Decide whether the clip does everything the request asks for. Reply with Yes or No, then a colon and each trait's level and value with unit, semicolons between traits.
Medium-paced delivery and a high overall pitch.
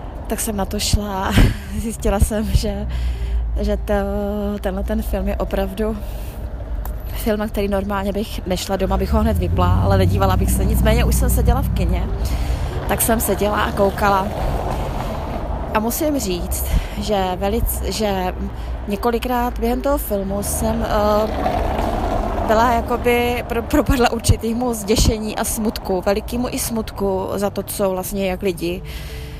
Yes: average, 140 wpm; high, 200 Hz